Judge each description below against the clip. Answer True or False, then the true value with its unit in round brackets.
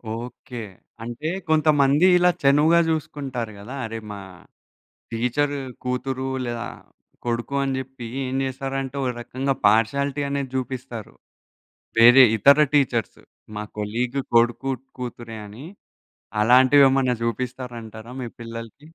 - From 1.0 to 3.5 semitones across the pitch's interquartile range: True (2.8 semitones)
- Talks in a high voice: False (130 Hz)